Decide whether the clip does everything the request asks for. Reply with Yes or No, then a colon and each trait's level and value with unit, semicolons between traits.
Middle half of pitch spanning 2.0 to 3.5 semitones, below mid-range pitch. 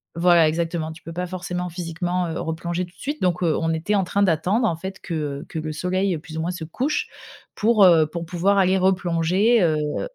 No: narrow, 2.5 semitones; medium, 175 Hz